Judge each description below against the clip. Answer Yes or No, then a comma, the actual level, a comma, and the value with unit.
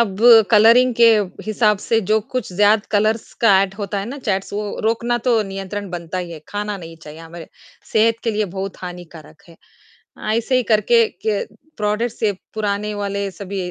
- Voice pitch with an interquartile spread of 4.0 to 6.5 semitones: No, average, 2.7 semitones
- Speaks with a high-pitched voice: Yes, high, 205 Hz